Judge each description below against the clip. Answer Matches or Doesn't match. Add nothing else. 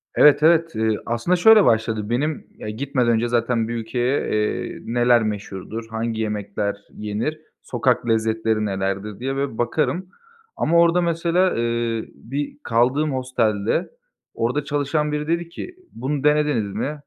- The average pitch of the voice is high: Doesn't match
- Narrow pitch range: Doesn't match